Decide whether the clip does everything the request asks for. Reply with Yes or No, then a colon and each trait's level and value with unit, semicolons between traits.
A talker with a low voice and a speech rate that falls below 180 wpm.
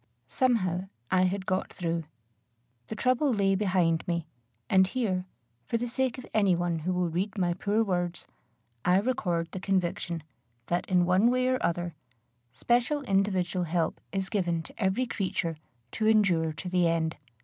No: medium, 185 Hz; average, 160 wpm